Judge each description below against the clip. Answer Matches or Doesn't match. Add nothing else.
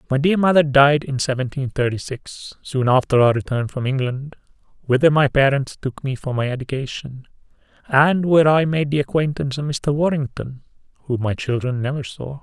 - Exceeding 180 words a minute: Doesn't match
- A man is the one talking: Matches